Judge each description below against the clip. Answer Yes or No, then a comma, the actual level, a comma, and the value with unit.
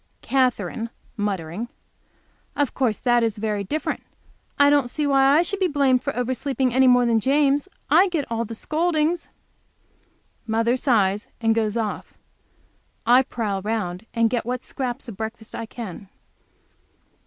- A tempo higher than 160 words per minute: No, average, 150 wpm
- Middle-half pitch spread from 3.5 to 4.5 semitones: Yes, average, 3.8 semitones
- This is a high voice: Yes, high, 240 Hz